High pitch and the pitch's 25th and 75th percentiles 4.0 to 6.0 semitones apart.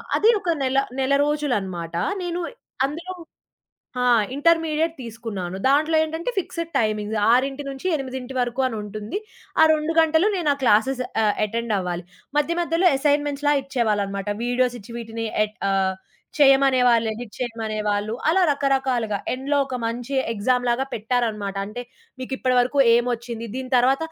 Yes: very high, 250 Hz; average, 4.7 semitones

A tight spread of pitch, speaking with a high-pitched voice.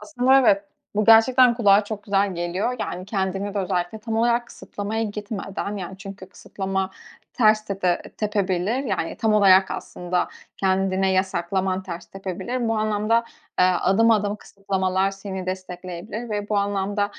Yes: narrow, 2.2 semitones; high, 200 Hz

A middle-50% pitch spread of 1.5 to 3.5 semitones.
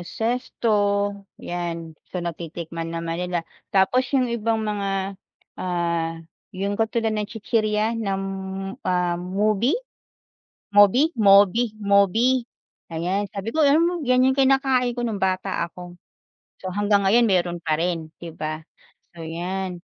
No: average, 4.6 semitones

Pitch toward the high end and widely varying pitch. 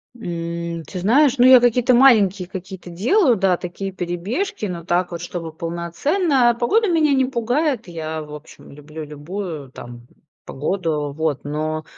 No: medium, 180 Hz; wide, 7.1 semitones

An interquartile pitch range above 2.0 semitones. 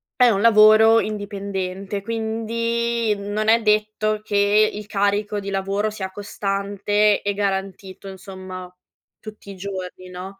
No: narrow, 1.7 semitones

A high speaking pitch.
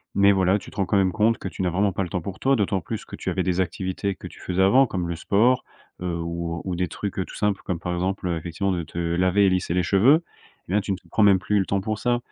No: very low, 95 Hz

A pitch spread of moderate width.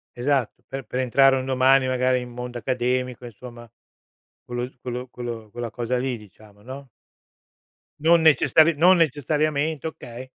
No: narrow, 2.2 semitones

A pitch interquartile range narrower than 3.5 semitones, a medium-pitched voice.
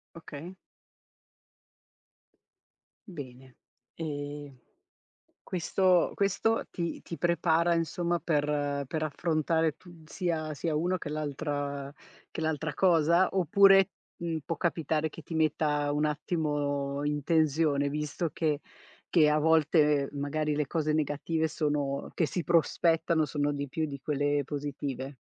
Yes: narrow, 2.5 semitones; medium, 155 Hz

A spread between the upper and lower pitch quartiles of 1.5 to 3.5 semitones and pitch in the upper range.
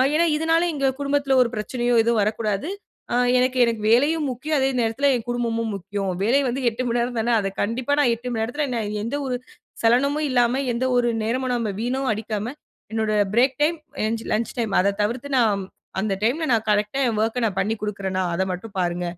Yes: average, 3.2 semitones; high, 235 Hz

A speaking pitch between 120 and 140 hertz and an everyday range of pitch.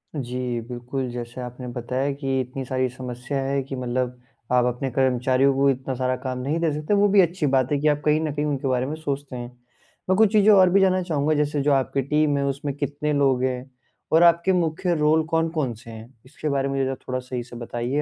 Yes: low, 135 Hz; average, 3.1 semitones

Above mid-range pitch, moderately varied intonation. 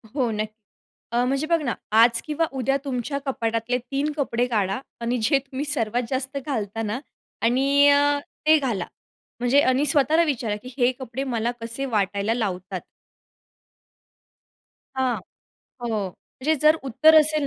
Yes: very high, 255 Hz; average, 3.6 semitones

